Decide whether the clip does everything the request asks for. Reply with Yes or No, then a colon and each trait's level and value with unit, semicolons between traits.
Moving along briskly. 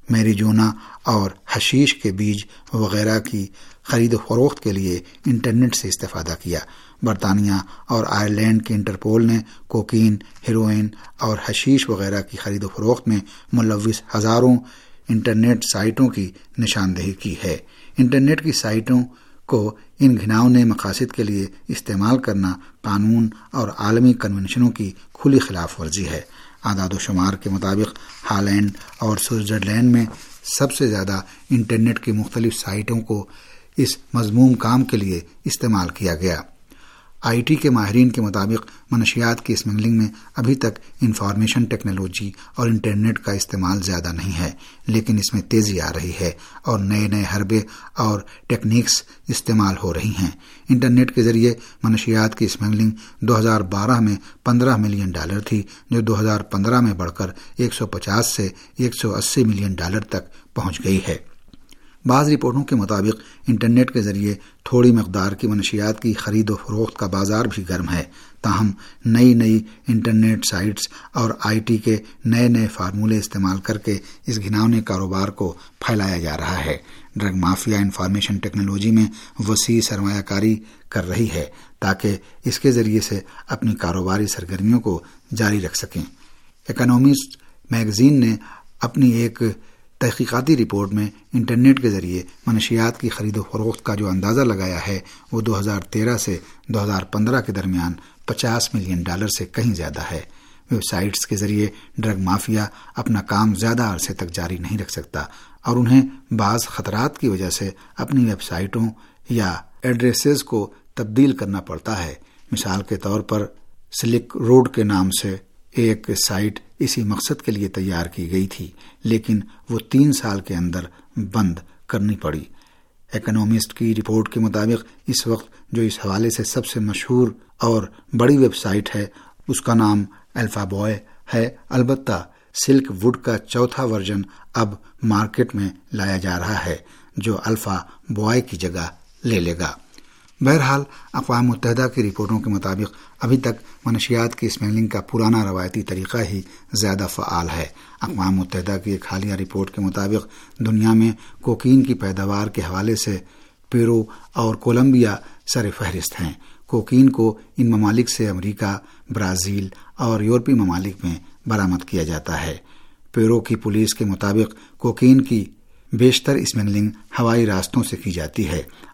No: average, 155 wpm